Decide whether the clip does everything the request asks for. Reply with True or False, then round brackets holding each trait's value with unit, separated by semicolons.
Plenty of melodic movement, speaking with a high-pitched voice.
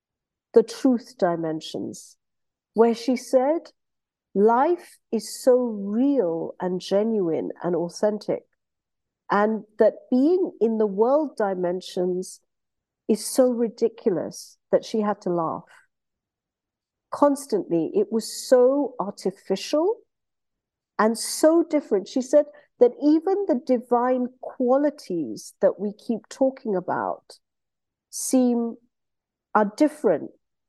True (5.8 semitones; 230 Hz)